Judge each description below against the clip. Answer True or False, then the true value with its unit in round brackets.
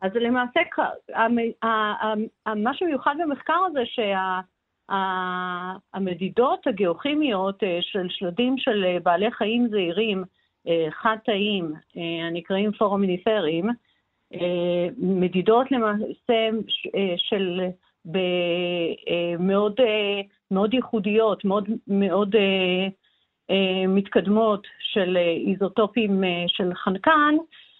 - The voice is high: True (200 Hz)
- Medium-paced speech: False (70 wpm)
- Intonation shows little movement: False (3.7 semitones)